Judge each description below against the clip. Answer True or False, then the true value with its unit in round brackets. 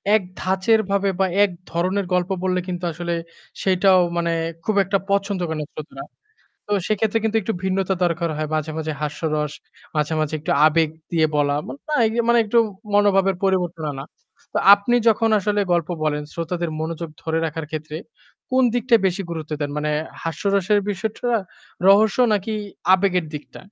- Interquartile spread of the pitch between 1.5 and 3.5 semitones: False (4.1 semitones)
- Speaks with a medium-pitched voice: True (180 Hz)